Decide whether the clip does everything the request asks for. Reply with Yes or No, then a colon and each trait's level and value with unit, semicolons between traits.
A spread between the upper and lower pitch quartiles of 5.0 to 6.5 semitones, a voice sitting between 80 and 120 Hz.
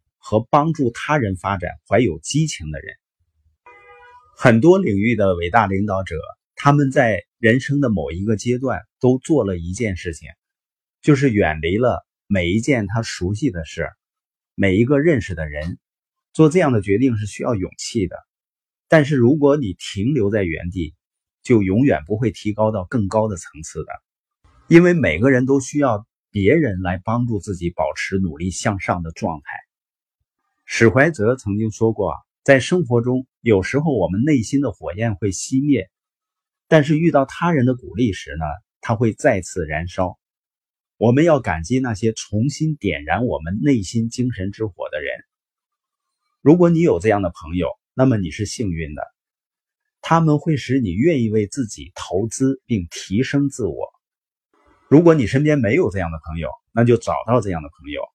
No: wide, 6.9 semitones; low, 115 Hz